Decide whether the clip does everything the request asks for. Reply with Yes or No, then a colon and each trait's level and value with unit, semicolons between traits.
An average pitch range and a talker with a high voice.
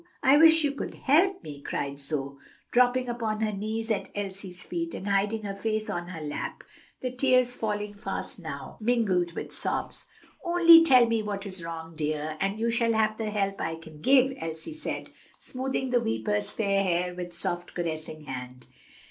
No: wide, 6.6 semitones; high, 205 Hz